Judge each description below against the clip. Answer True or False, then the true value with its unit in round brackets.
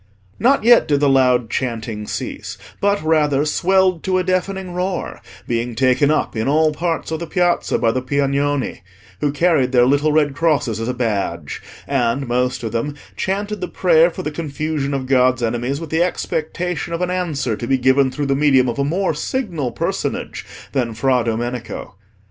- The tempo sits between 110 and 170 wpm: False (185 wpm)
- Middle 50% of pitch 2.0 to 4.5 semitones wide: False (5.0 semitones)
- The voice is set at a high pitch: False (140 Hz)